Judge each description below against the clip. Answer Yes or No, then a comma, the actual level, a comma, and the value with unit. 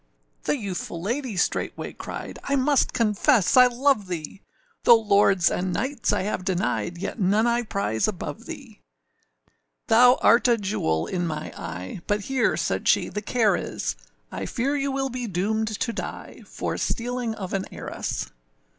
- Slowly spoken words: No, average, 165 wpm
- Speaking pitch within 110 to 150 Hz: No, high, 215 Hz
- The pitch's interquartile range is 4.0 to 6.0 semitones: Yes, average, 4.8 semitones